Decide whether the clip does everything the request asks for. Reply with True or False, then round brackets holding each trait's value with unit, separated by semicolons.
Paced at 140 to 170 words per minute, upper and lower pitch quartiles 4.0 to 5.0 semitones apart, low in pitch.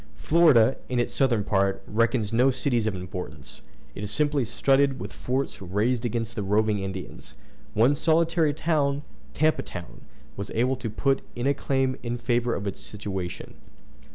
True (160 wpm; 4.7 semitones; 120 Hz)